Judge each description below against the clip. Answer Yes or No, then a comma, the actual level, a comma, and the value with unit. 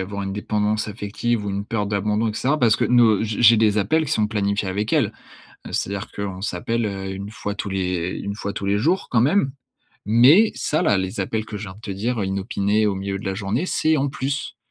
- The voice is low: Yes, low, 105 Hz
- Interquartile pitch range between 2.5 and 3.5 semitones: Yes, average, 2.8 semitones